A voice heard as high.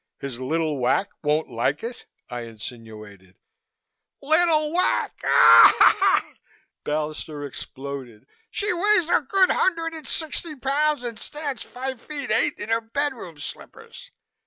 Yes: high, 225 Hz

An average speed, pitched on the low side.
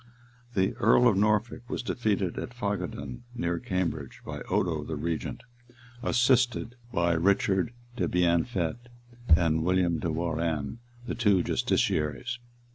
No: slow, 120 wpm; very low, 95 Hz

